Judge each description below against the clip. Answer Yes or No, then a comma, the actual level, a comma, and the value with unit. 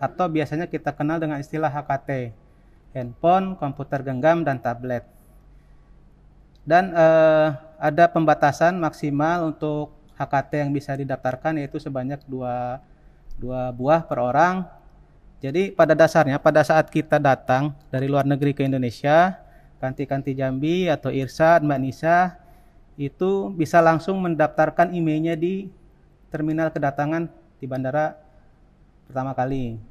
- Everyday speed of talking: Yes, average, 120 wpm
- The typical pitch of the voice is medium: Yes, medium, 150 Hz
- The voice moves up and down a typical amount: Yes, average, 3.2 semitones